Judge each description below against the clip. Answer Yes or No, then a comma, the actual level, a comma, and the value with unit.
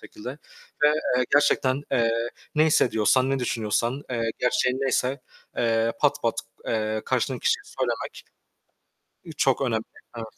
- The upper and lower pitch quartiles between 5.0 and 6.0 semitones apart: No, average, 2.9 semitones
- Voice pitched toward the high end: No, low, 125 Hz